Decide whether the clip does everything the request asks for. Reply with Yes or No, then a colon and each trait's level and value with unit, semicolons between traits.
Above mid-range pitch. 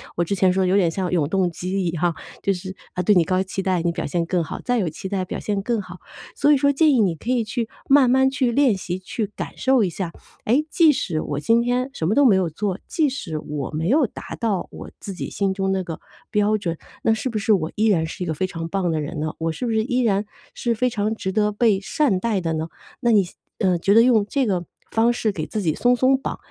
Yes: high, 200 Hz